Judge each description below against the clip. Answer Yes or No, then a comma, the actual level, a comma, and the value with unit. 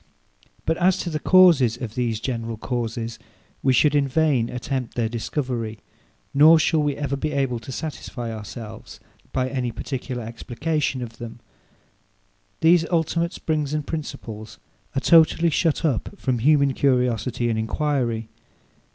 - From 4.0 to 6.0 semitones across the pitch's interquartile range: Yes, average, 4.6 semitones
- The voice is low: Yes, low, 130 Hz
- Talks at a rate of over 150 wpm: No, average, 145 wpm